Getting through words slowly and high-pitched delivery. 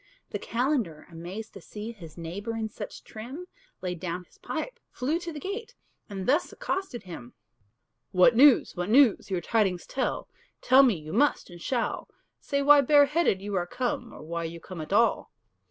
No: average, 180 wpm; high, 220 Hz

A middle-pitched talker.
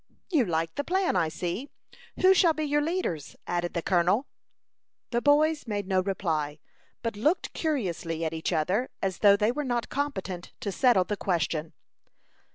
No: high, 200 Hz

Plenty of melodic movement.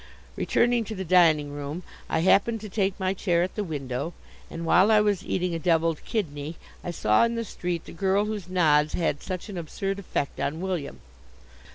No: average, 3.7 semitones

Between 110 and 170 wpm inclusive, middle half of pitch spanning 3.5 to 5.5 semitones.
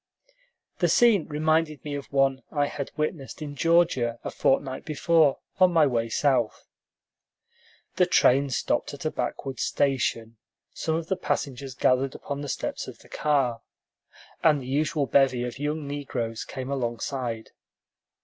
No: average, 150 wpm; average, 3.0 semitones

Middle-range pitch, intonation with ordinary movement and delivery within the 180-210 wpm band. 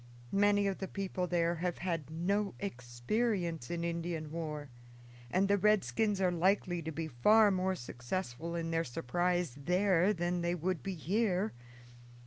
No: medium, 175 Hz; average, 3.1 semitones; average, 150 wpm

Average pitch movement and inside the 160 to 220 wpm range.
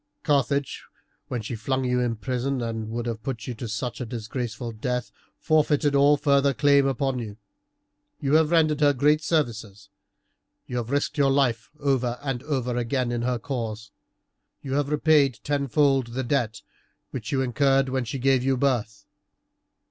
Yes: average, 3.0 semitones; average, 165 wpm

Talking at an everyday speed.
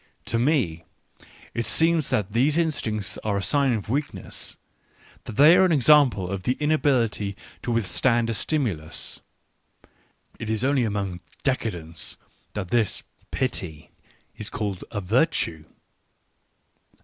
No: slow, 125 wpm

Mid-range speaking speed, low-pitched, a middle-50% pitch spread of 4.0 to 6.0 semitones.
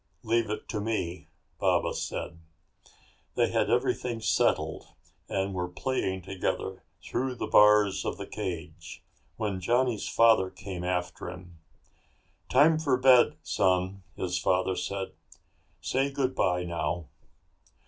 No: slow, 120 wpm; very low, 95 Hz; average, 4.7 semitones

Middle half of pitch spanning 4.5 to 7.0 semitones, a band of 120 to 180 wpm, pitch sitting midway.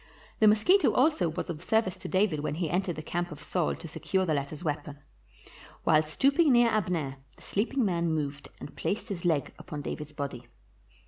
No: wide, 5.5 semitones; average, 195 wpm; medium, 170 Hz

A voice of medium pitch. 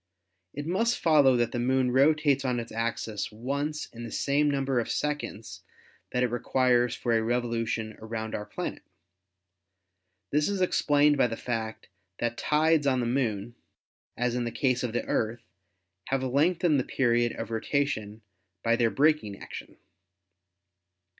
No: low, 125 Hz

